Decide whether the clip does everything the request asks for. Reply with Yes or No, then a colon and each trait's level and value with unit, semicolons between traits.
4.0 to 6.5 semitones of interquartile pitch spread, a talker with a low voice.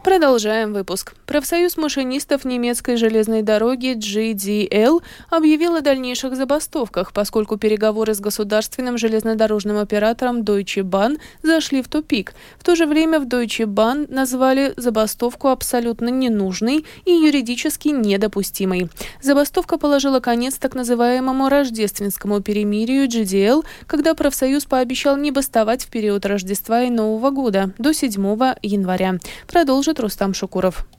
No: average, 4.7 semitones; high, 245 Hz